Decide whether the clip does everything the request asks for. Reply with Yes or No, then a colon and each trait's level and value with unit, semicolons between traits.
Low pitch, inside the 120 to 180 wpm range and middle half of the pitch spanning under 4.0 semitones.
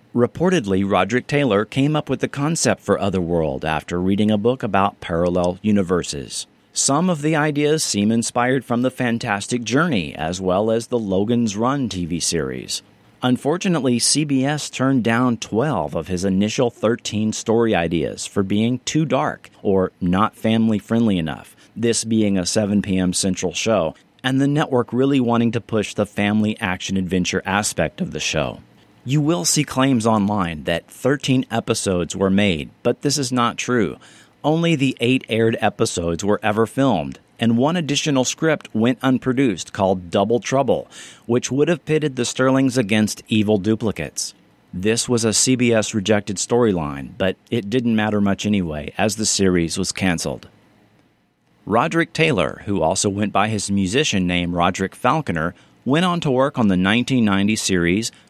No: low, 110 Hz; average, 160 wpm; average, 4.8 semitones